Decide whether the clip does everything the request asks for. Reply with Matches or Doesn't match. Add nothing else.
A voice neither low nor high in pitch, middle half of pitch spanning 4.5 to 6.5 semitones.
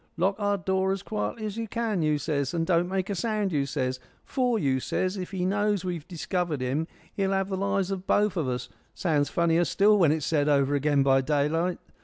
Matches